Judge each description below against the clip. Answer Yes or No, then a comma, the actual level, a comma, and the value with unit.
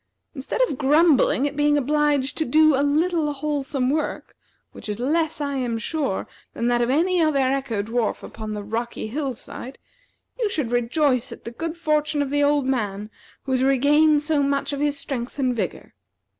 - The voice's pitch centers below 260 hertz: No, very high, 280 Hz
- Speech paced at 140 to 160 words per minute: No, average, 185 wpm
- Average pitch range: Yes, average, 3.6 semitones